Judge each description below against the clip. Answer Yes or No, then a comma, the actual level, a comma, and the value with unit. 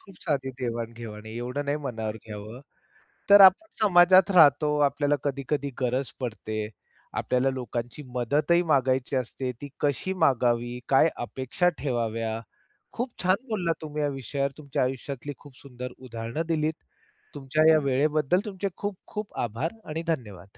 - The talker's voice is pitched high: No, low, 135 Hz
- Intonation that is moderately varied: Yes, average, 4.2 semitones